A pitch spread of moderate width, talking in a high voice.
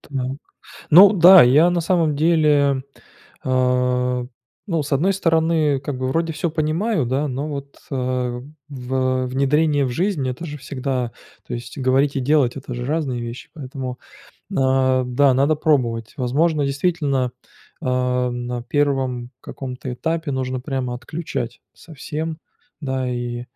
No: average, 3.5 semitones; low, 135 Hz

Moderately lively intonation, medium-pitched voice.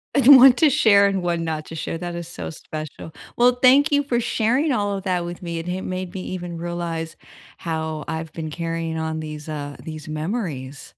Yes: average, 4.0 semitones; medium, 170 Hz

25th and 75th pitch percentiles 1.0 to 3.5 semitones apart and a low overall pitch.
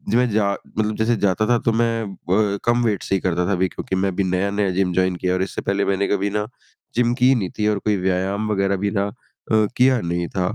Yes: average, 2.7 semitones; low, 100 Hz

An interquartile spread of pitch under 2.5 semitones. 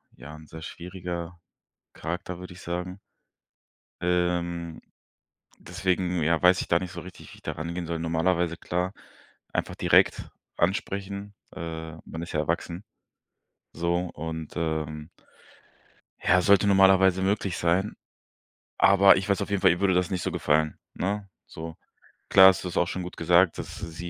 Yes: narrow, 2.0 semitones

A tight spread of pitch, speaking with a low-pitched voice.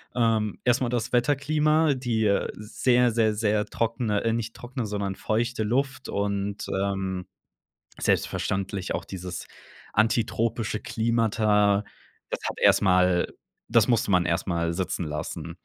No: average, 3.2 semitones; low, 110 Hz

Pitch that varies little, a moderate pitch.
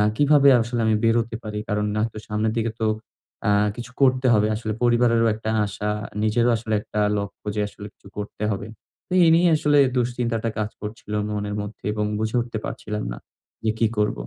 No: narrow, 2.1 semitones; low, 110 Hz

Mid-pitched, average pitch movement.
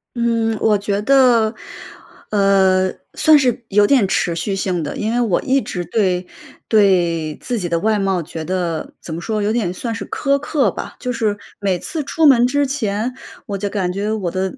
No: high, 205 Hz; average, 4.3 semitones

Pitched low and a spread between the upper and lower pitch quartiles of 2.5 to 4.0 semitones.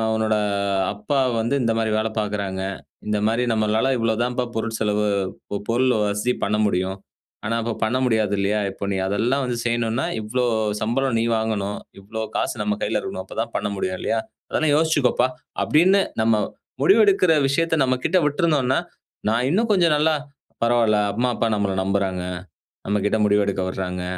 Yes: low, 110 Hz; average, 3.7 semitones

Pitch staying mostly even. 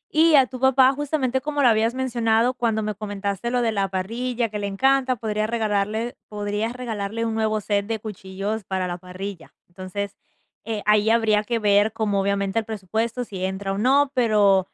No: average, 3.0 semitones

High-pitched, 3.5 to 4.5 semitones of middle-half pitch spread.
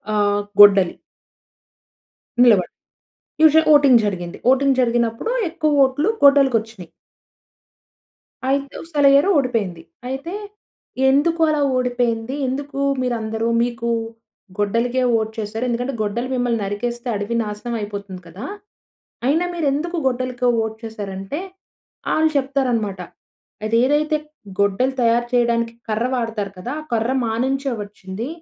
Yes: high, 240 Hz; average, 4.1 semitones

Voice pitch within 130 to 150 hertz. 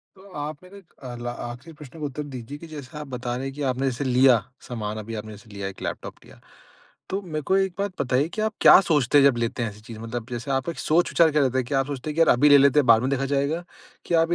Yes: low, 135 Hz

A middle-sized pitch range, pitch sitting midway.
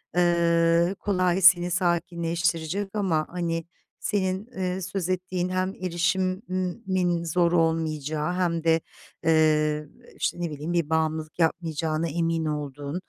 No: narrow, 2.3 semitones; medium, 170 Hz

